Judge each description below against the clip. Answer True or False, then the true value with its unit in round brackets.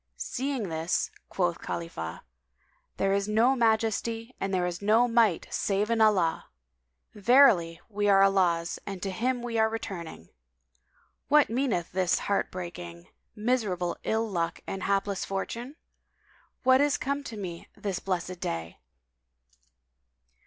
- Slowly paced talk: True (130 wpm)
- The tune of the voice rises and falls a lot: False (4.5 semitones)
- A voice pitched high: True (200 Hz)